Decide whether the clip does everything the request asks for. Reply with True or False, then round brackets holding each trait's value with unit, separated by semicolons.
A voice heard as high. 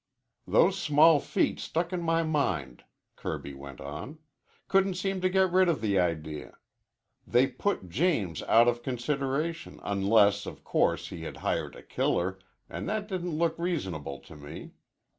False (140 Hz)